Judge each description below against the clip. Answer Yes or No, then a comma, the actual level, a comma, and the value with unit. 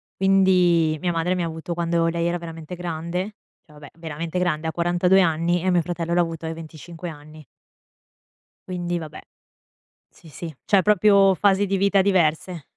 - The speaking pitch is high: No, medium, 170 Hz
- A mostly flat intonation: Yes, narrow, 2.0 semitones